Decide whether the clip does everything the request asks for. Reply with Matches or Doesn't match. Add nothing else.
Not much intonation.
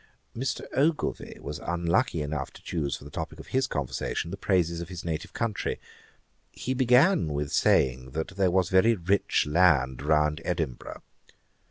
Doesn't match